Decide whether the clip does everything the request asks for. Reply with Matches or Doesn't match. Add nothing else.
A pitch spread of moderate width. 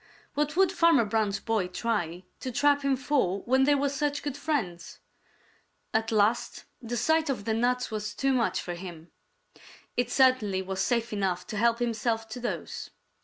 Matches